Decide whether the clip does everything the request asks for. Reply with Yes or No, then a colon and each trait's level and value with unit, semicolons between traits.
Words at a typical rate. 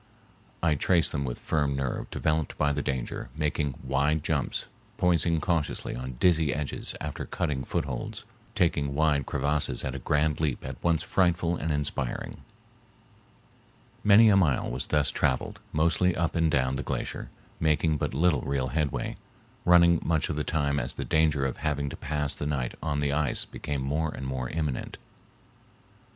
Yes: average, 165 wpm